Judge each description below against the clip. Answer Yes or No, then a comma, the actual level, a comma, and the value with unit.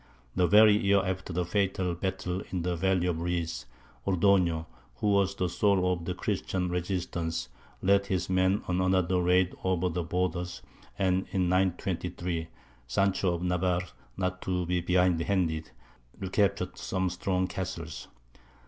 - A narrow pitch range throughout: Yes, narrow, 1.2 semitones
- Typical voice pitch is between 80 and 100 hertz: Yes, very low, 90 Hz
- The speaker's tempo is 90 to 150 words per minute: Yes, average, 140 wpm